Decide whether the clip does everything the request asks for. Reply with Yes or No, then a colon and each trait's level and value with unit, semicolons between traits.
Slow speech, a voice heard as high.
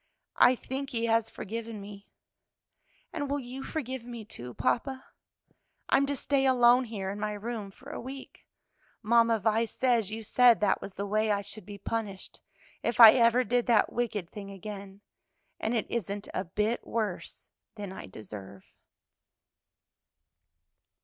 No: average, 155 wpm; high, 225 Hz